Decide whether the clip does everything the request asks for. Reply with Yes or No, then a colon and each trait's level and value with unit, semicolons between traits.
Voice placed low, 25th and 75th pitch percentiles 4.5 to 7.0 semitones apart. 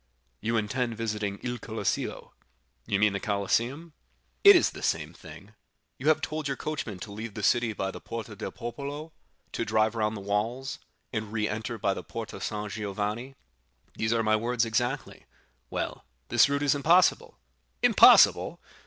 No: low, 115 Hz; average, 4.0 semitones